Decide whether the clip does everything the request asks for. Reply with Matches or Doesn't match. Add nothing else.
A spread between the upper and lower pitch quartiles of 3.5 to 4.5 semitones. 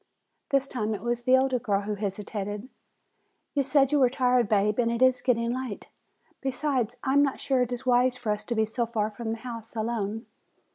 Doesn't match